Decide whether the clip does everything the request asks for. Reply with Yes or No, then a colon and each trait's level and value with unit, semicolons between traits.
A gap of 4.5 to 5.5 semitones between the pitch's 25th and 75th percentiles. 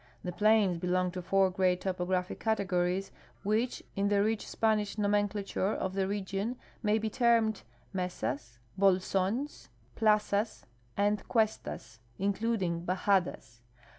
No: average, 2.7 semitones